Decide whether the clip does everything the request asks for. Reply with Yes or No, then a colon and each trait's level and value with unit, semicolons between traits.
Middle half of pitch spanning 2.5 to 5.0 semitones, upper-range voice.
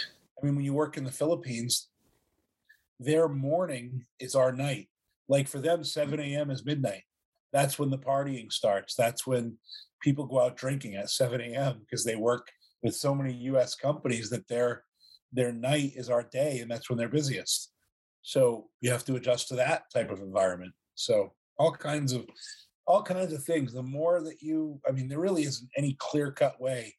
No: average, 3.2 semitones; low, 135 Hz